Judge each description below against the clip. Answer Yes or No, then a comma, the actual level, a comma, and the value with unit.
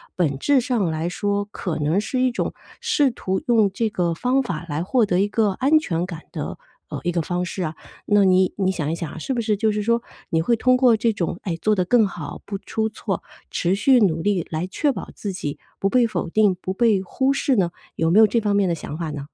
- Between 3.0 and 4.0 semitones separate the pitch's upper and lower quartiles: No, average, 5.0 semitones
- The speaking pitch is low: No, high, 200 Hz